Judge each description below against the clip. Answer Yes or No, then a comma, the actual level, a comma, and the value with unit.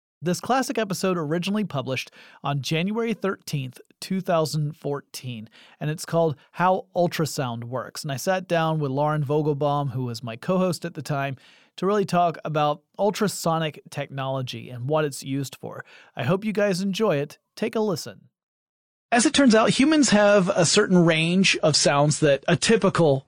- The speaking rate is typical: Yes, average, 165 wpm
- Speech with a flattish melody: No, average, 5.2 semitones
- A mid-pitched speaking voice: Yes, medium, 165 Hz